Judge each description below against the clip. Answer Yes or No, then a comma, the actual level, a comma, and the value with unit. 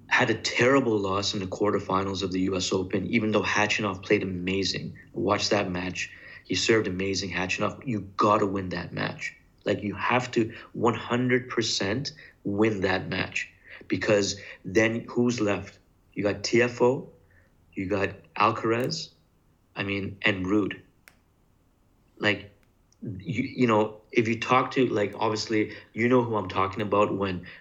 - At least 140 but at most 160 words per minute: Yes, average, 145 wpm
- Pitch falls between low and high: No, low, 105 Hz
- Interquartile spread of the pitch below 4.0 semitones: Yes, average, 2.7 semitones